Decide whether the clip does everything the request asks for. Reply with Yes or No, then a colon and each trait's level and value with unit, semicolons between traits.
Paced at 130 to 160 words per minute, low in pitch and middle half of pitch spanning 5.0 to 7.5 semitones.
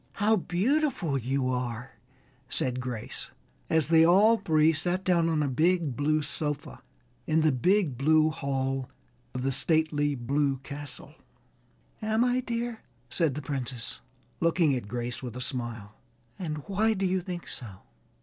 No: average, 150 wpm; medium, 150 Hz; wide, 5.5 semitones